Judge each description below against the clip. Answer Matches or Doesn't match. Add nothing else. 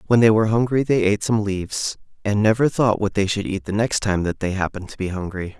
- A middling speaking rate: Doesn't match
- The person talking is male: Matches